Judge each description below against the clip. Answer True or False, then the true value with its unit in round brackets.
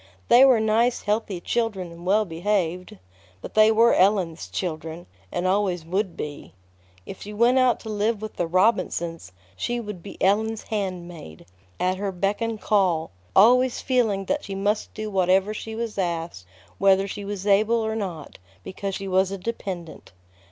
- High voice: True (195 Hz)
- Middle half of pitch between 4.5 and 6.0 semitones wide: False (3.4 semitones)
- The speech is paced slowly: False (165 wpm)